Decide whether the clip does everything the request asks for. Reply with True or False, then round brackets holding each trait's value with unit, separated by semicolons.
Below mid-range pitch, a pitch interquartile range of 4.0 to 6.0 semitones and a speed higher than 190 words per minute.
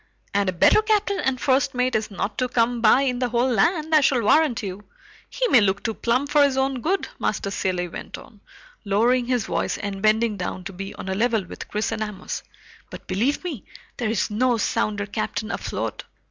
False (230 Hz; 4.4 semitones; 200 wpm)